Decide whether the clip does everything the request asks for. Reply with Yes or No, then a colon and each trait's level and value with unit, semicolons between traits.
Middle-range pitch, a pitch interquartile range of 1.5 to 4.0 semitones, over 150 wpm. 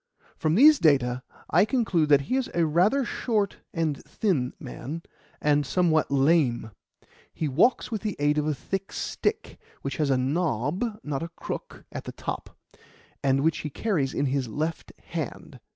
No: medium, 155 Hz; average, 5.3 semitones; average, 170 wpm